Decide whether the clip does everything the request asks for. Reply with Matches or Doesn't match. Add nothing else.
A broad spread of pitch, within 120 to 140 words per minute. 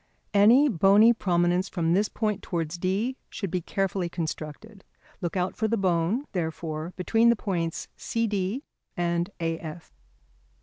Doesn't match